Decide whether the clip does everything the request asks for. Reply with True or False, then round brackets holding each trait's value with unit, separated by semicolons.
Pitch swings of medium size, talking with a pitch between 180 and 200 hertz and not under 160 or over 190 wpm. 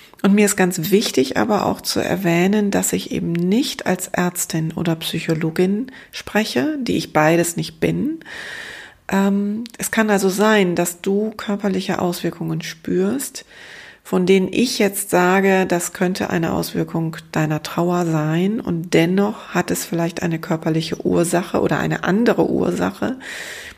False (3.2 semitones; 185 Hz; 145 wpm)